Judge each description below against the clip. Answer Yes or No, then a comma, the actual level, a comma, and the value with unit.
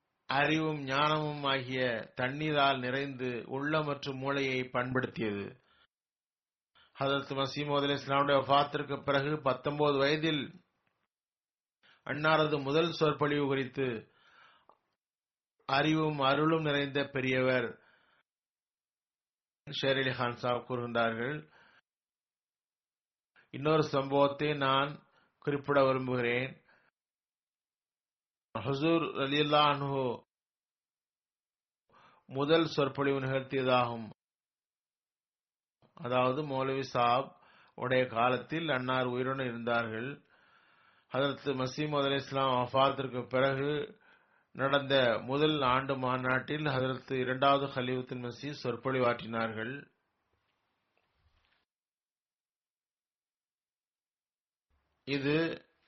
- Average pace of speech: No, slow, 55 wpm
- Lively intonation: No, narrow, 2.2 semitones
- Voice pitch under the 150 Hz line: Yes, low, 135 Hz